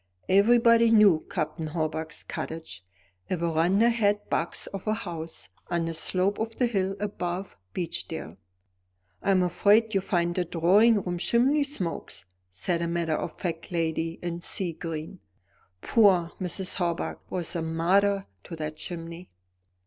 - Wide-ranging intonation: No, average, 3.5 semitones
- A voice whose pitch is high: No, medium, 175 Hz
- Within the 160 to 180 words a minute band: No, average, 140 wpm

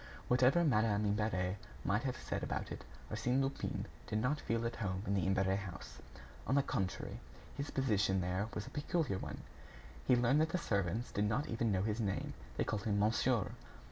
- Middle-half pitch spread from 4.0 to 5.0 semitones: Yes, average, 4.4 semitones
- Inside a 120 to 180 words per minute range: No, average, 190 wpm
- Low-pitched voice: Yes, low, 110 Hz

